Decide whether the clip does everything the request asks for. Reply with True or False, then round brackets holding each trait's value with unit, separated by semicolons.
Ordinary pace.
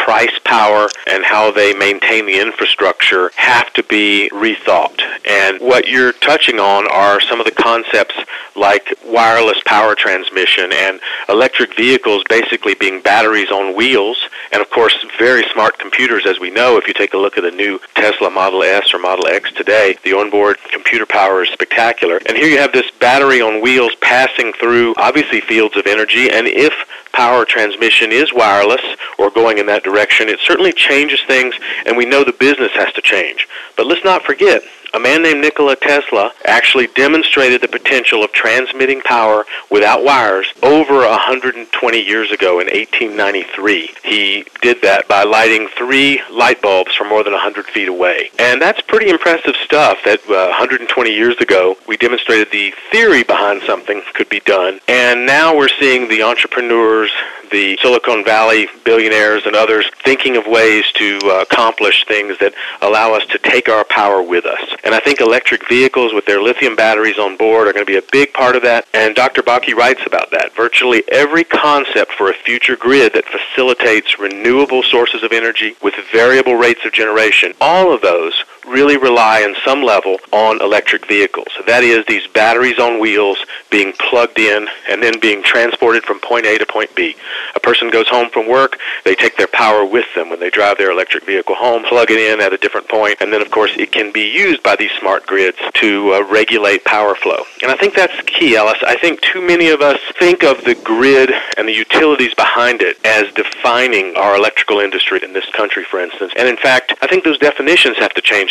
True (190 wpm)